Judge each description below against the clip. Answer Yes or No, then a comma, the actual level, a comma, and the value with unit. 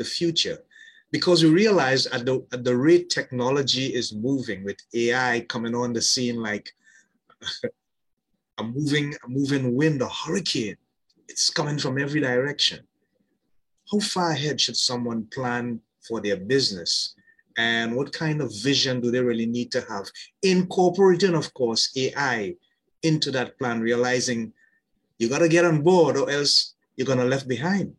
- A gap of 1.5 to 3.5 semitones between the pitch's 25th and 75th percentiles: No, average, 4.5 semitones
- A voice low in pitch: Yes, low, 130 Hz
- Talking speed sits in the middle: Yes, average, 155 wpm